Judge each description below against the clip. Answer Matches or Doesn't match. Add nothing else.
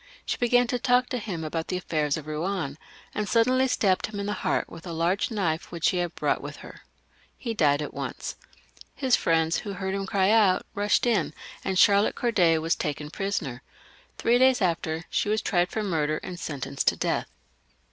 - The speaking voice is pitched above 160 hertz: Matches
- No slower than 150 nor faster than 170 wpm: Doesn't match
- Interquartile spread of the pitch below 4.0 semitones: Doesn't match